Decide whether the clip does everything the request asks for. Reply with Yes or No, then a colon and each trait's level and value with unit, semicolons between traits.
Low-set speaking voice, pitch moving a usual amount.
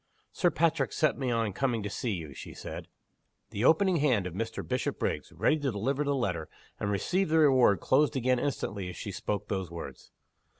No: low, 120 Hz; wide, 6.2 semitones